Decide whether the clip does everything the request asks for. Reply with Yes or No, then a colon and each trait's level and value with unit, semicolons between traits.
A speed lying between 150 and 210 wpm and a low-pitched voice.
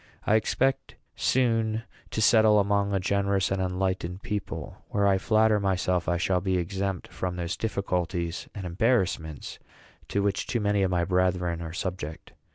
Yes: average, 160 wpm; very low, 95 Hz